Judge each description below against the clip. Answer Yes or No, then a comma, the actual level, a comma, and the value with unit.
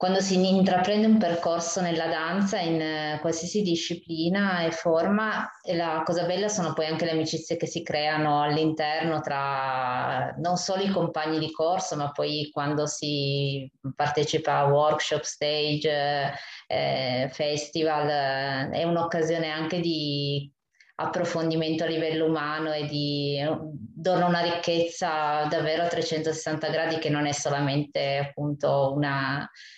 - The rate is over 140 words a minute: No, average, 130 wpm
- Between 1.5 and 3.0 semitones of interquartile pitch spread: Yes, narrow, 2.4 semitones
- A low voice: No, medium, 155 Hz